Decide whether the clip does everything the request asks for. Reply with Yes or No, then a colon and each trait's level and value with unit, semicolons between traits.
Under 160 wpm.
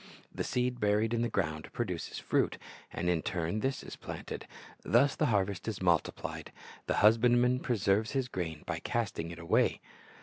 No: average, 170 wpm